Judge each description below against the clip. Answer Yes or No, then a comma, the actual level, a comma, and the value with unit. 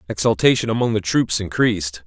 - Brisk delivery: No, average, 145 wpm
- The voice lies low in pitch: Yes, low, 105 Hz